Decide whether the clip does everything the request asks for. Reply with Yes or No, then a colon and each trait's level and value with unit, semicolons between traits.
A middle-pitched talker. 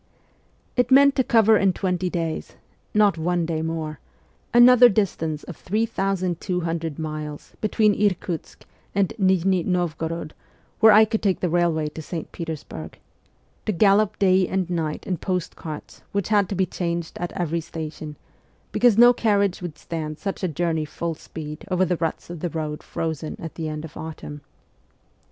Yes: medium, 175 Hz